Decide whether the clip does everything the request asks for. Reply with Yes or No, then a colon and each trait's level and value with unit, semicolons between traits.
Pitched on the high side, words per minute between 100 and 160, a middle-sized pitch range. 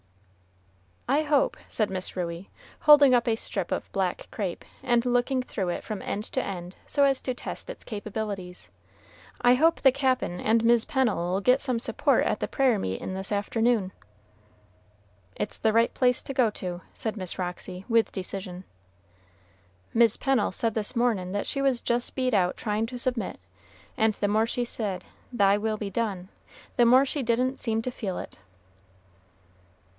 No: high, 225 Hz; average, 170 wpm; average, 4.3 semitones